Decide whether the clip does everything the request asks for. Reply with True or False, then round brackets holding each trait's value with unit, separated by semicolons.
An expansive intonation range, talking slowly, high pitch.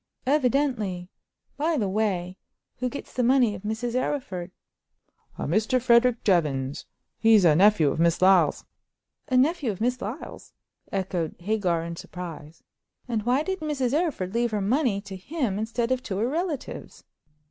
False (5.7 semitones; 155 wpm; 220 Hz)